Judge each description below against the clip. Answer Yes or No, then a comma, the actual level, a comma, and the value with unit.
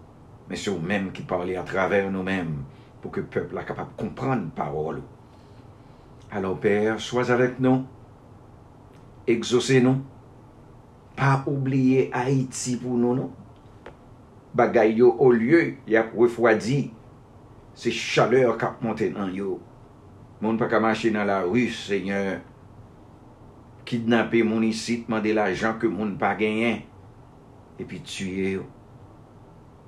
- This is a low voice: Yes, low, 115 Hz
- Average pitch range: Yes, average, 3.1 semitones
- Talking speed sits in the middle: No, slow, 130 wpm